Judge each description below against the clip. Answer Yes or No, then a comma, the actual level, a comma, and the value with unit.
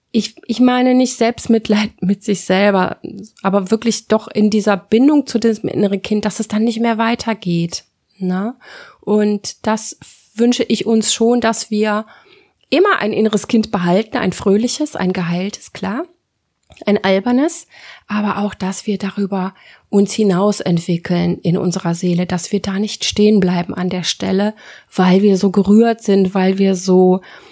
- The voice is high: Yes, high, 210 Hz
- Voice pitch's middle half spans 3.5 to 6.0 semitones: No, average, 3.1 semitones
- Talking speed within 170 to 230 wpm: No, average, 160 wpm